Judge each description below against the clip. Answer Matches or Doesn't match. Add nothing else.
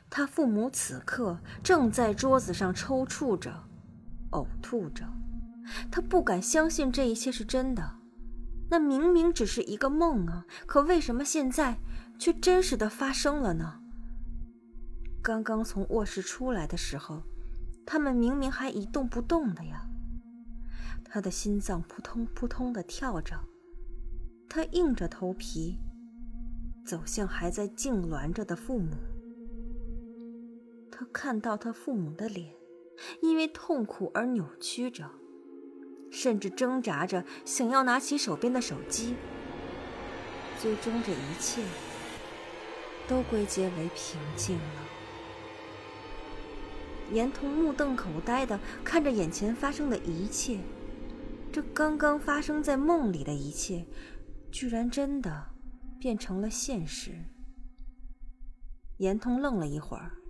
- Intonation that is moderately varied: Doesn't match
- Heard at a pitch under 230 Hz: Doesn't match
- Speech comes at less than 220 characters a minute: Matches